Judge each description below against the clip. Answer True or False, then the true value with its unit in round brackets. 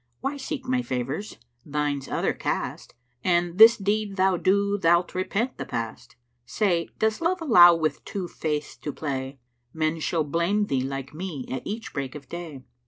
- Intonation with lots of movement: True (6.0 semitones)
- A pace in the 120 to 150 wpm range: False (170 wpm)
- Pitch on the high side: False (170 Hz)